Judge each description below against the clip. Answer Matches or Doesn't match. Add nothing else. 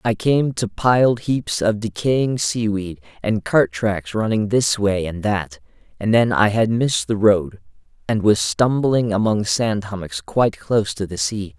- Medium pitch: Doesn't match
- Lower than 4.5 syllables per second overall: Matches